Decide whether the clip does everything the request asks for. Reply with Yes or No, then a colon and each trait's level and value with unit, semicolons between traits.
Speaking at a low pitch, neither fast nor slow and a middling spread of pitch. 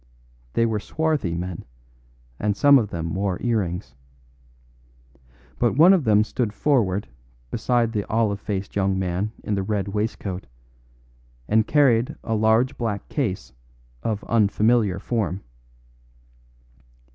No: low, 105 Hz; slow, 125 wpm; average, 3.1 semitones